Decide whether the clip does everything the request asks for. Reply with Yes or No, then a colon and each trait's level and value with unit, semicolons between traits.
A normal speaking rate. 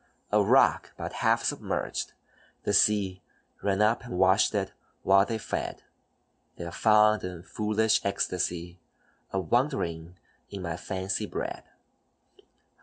No: slow, 120 wpm